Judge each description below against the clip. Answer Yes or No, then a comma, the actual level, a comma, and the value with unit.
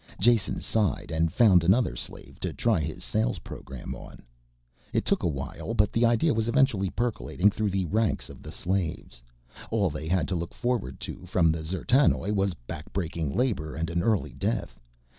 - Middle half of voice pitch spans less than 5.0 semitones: No, average, 5.3 semitones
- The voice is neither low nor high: No, very low, 95 Hz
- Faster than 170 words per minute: Yes, average, 180 wpm